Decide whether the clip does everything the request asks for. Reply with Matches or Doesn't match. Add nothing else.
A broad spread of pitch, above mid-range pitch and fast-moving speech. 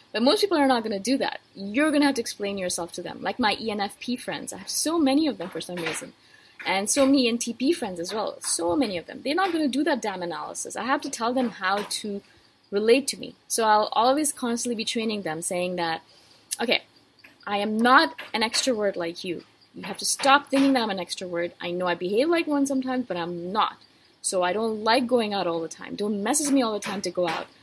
Matches